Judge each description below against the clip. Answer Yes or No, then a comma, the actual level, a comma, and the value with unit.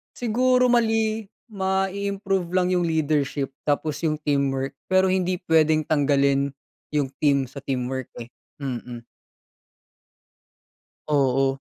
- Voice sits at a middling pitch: Yes, medium, 155 Hz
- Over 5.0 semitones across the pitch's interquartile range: Yes, wide, 5.6 semitones